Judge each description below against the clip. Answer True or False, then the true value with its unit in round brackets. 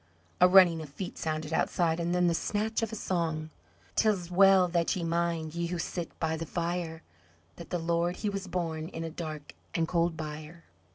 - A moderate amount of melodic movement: False (1.8 semitones)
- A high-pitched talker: False (170 Hz)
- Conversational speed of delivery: True (195 wpm)